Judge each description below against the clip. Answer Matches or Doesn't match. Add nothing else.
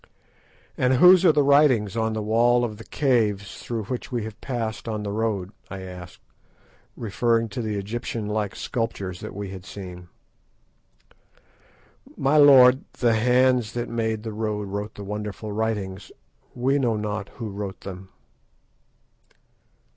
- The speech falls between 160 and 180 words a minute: Doesn't match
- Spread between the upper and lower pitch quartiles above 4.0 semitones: Doesn't match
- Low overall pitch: Matches